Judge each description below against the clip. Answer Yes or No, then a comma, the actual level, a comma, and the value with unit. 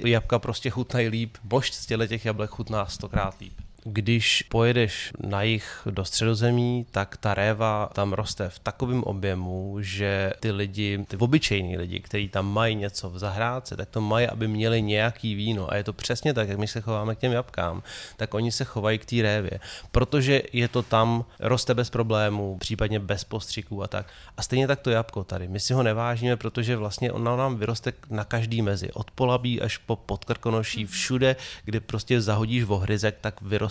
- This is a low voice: Yes, low, 110 Hz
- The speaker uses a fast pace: Yes, fast, 185 wpm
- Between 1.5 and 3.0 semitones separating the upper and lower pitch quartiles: Yes, average, 2.7 semitones